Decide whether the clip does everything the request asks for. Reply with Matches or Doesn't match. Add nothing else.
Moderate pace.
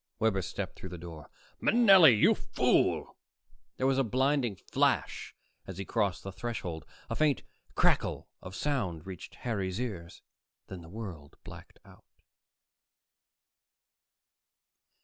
Doesn't match